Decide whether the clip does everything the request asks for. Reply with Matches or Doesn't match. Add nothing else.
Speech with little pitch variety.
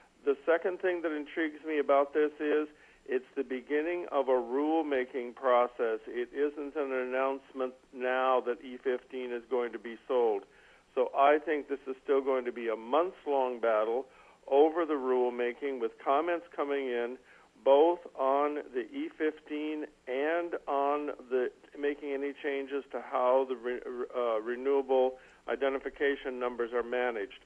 Doesn't match